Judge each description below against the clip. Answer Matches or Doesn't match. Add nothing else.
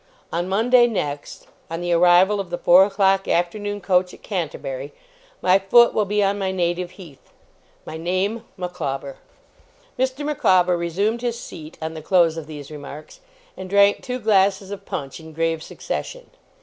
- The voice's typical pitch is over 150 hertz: Matches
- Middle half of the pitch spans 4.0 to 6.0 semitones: Doesn't match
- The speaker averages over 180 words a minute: Doesn't match